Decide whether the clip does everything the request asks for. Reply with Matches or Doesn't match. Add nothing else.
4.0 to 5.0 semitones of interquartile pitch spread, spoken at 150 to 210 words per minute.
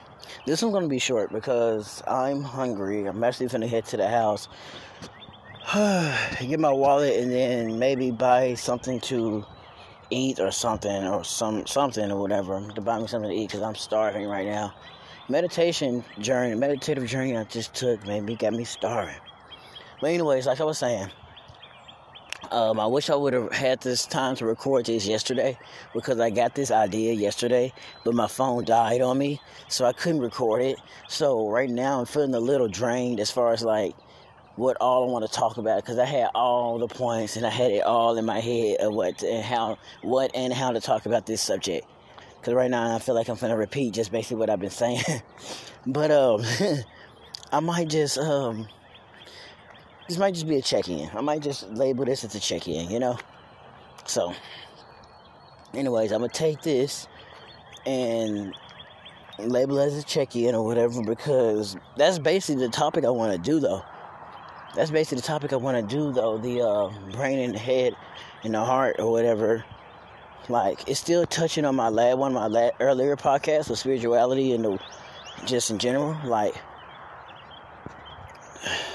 Doesn't match